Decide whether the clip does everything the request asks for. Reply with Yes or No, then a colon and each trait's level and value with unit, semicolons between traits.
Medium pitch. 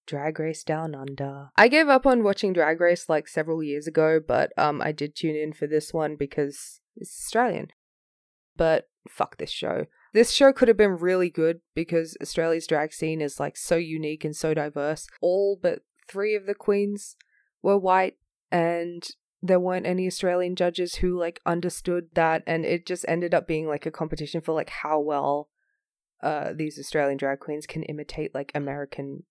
Yes: medium, 165 Hz